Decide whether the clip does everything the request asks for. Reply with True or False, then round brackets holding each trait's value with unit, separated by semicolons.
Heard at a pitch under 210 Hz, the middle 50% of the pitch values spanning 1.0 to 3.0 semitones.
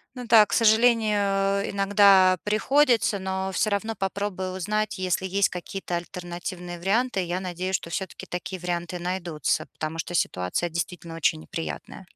True (190 Hz; 2.7 semitones)